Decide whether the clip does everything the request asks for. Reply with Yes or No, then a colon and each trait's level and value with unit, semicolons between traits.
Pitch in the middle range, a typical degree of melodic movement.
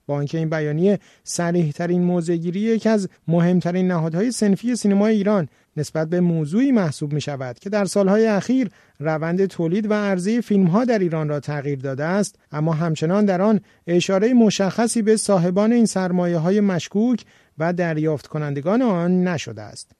Yes: medium, 180 Hz; average, 4.4 semitones